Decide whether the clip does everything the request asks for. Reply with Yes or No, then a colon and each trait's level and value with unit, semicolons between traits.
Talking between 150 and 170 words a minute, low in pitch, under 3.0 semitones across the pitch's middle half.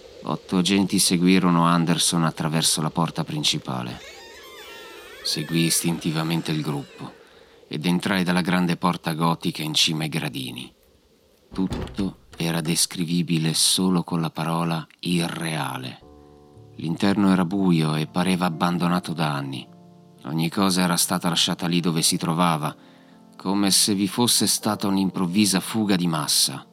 No: average, 125 wpm; very low, 85 Hz; narrow, 2.6 semitones